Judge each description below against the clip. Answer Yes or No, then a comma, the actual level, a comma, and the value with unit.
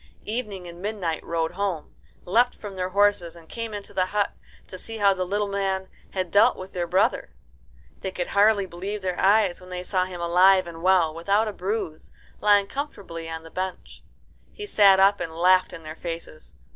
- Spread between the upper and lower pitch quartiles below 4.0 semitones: Yes, average, 2.7 semitones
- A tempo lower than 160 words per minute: No, average, 195 wpm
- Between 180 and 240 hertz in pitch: Yes, high, 190 Hz